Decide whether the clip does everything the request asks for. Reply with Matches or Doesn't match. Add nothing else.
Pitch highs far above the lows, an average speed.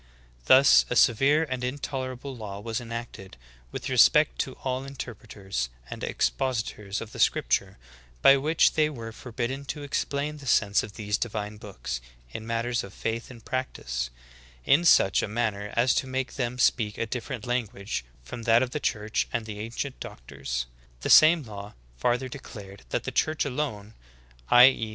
Doesn't match